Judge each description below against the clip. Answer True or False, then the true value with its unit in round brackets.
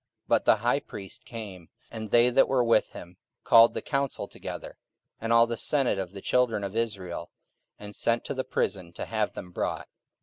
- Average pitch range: True (3.5 semitones)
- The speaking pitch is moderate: False (115 Hz)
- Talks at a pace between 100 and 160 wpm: False (200 wpm)